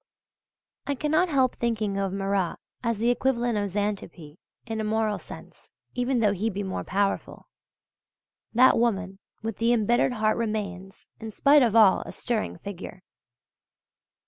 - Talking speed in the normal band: Yes, average, 145 wpm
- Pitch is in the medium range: No, high, 220 Hz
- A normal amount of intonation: Yes, average, 3.2 semitones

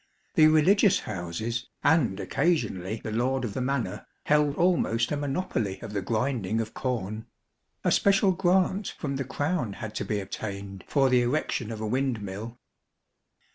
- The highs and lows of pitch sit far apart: Yes, wide, 5.7 semitones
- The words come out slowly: No, average, 155 wpm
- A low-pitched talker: Yes, low, 120 Hz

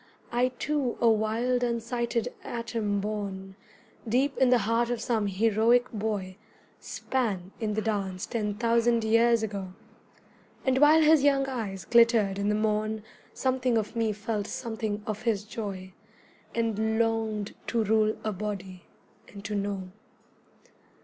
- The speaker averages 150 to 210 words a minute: No, average, 140 wpm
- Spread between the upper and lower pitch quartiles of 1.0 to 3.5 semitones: Yes, narrow, 2.4 semitones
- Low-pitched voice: No, high, 220 Hz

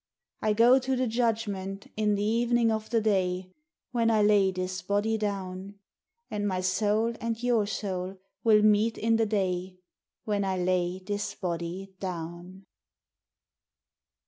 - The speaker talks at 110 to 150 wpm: Yes, average, 145 wpm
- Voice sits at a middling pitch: No, high, 205 Hz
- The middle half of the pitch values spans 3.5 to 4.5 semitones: No, average, 3.0 semitones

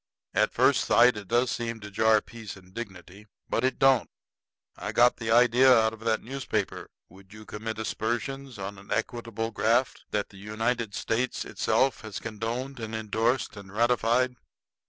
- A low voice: Yes, low, 115 Hz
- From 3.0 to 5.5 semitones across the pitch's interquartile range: No, narrow, 2.4 semitones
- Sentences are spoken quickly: No, average, 165 wpm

